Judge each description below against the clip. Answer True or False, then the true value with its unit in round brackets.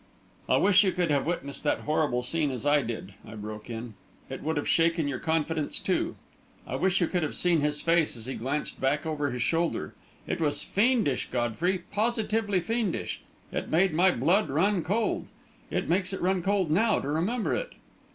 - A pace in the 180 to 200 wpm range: True (190 wpm)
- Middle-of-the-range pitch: True (165 Hz)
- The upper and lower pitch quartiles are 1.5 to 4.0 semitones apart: False (4.9 semitones)